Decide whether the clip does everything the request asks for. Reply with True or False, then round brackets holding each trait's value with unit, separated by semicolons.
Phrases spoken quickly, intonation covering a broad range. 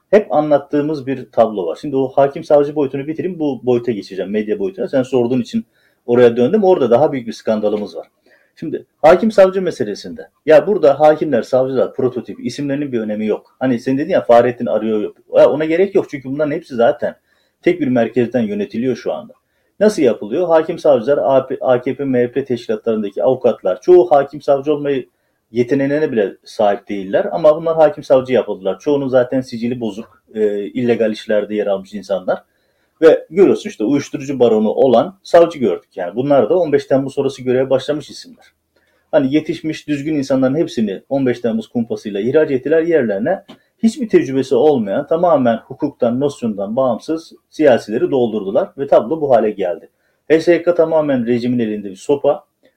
False (155 wpm; 4.4 semitones)